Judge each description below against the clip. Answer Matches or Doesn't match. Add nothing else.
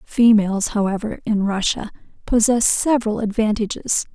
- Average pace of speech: Doesn't match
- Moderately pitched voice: Doesn't match